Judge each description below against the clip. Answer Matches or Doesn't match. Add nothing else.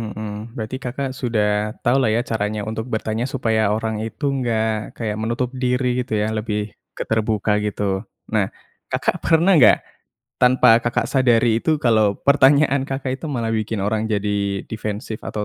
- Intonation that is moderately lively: Matches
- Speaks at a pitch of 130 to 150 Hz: Doesn't match